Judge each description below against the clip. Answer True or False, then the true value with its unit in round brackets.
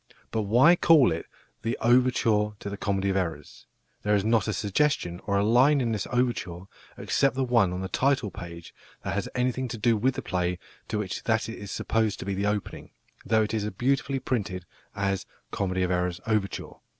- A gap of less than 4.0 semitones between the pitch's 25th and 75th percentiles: False (4.3 semitones)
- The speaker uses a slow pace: False (200 wpm)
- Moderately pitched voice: False (105 Hz)